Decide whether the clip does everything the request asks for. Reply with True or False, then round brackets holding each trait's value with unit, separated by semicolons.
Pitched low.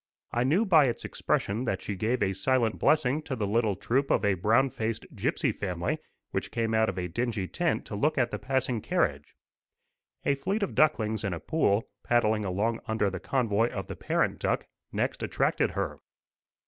True (115 Hz)